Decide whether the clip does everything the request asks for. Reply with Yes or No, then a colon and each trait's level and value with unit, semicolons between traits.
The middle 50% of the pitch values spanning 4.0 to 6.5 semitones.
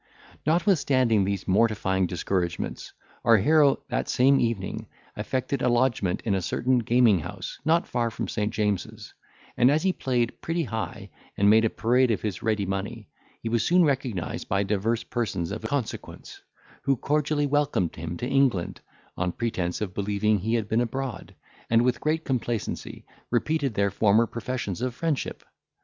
Yes: average, 4.6 semitones